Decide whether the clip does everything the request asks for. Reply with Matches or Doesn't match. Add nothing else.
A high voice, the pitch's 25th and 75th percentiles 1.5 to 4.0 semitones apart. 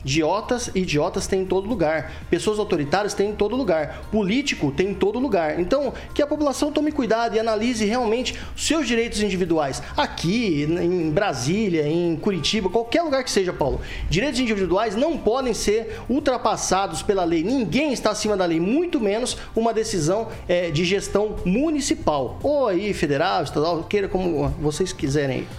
Doesn't match